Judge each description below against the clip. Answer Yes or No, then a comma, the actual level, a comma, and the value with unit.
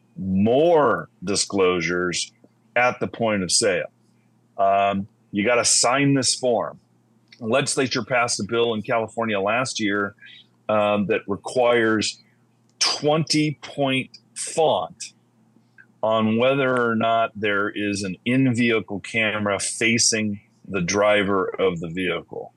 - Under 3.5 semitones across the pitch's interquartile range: Yes, average, 3.0 semitones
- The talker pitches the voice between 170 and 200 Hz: No, low, 110 Hz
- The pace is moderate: No, slow, 115 wpm